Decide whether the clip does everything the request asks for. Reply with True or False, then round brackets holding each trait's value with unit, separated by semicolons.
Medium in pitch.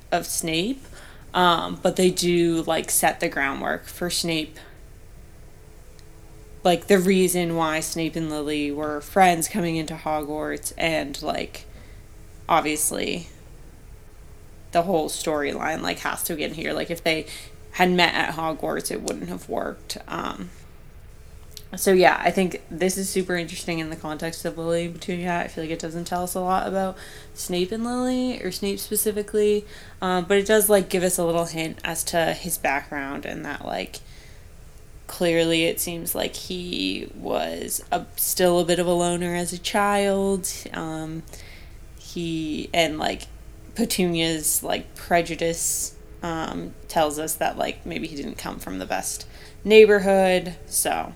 True (170 Hz)